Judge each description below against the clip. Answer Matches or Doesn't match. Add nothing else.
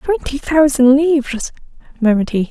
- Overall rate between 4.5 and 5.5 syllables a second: Matches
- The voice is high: Matches